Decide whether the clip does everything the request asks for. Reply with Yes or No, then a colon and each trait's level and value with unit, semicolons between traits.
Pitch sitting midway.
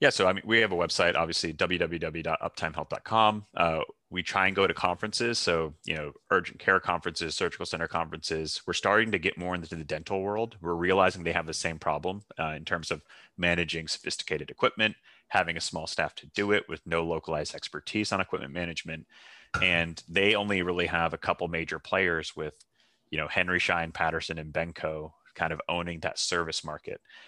No: very low, 85 Hz